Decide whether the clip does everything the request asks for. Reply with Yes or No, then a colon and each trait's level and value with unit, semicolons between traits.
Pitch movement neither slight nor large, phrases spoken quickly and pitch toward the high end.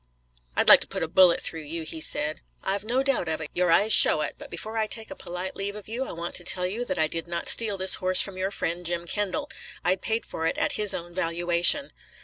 No: average, 3.7 semitones; fast, 260 wpm; medium, 180 Hz